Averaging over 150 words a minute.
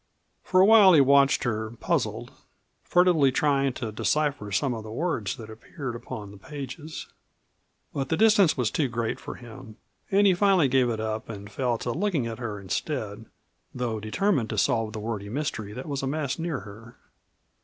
Yes: average, 180 wpm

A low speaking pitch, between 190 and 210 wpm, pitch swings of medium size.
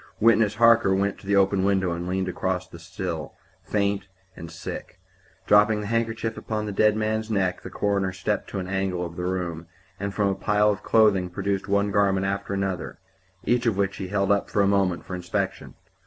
No: low, 100 Hz; average, 200 wpm; narrow, 1.9 semitones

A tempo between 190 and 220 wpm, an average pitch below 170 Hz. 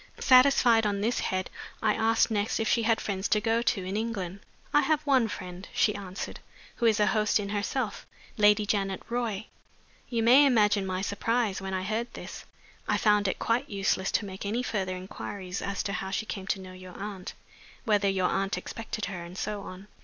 No: average, 200 wpm; high, 205 Hz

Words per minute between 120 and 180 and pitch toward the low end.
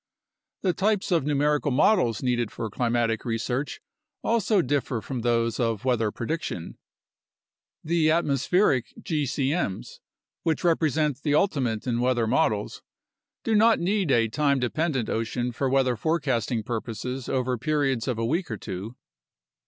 Yes: slow, 135 wpm; low, 130 Hz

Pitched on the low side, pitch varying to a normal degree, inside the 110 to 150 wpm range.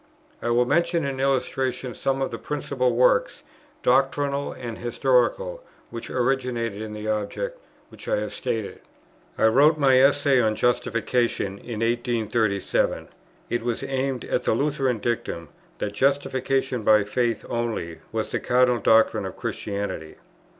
Yes: low, 125 Hz; average, 3.2 semitones; average, 140 wpm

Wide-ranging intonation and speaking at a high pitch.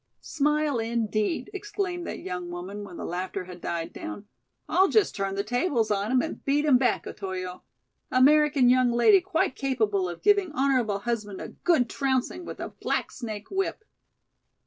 Yes: wide, 7.1 semitones; high, 245 Hz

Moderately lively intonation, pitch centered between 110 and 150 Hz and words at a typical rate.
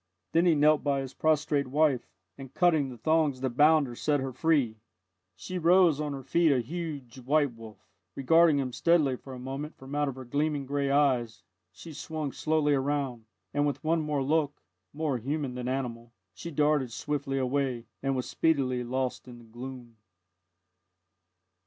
Yes: average, 3.1 semitones; medium, 140 Hz; average, 175 wpm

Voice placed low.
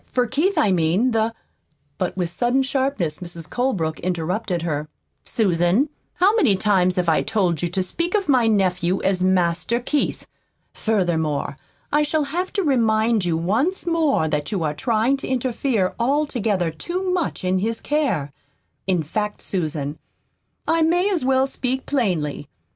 No: high, 215 Hz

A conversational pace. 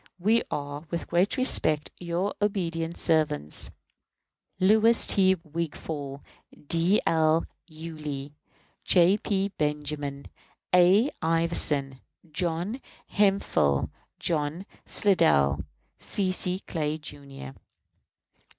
No: slow, 85 wpm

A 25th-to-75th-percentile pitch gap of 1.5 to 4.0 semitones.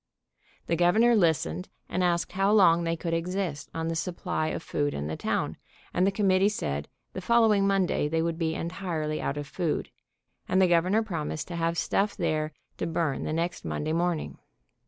Yes: average, 3.2 semitones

